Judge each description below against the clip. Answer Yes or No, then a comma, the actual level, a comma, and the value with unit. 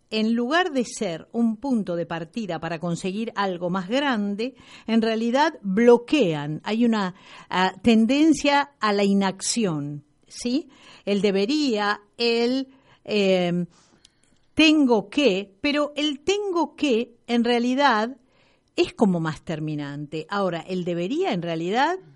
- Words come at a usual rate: No, slow, 120 wpm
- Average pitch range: No, wide, 6.1 semitones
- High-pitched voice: Yes, high, 225 Hz